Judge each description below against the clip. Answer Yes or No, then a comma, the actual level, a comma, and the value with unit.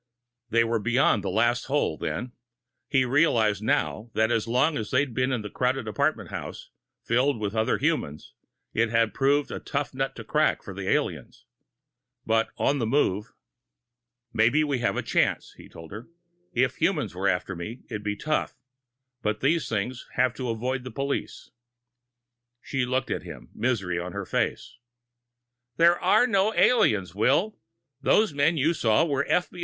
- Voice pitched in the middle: No, low, 125 Hz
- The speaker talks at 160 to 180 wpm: Yes, average, 170 wpm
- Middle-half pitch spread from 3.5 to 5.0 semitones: Yes, average, 4.4 semitones